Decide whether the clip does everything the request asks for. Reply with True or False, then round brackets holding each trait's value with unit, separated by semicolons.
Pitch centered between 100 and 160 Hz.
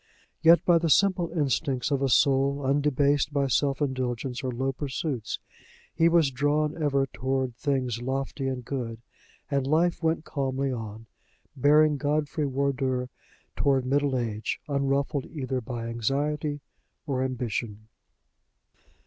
True (135 Hz)